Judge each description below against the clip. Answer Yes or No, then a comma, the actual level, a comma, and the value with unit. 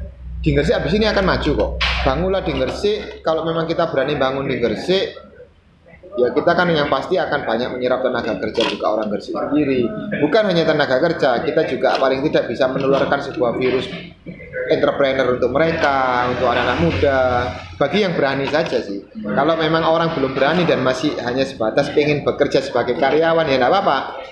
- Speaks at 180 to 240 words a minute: No, average, 170 wpm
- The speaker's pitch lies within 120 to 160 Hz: Yes, low, 135 Hz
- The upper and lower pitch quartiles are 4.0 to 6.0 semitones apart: Yes, average, 4.7 semitones